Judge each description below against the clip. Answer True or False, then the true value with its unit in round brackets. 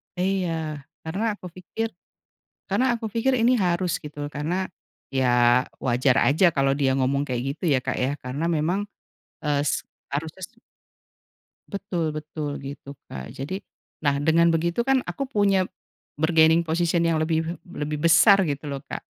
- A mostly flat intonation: False (4.5 semitones)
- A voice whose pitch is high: False (160 Hz)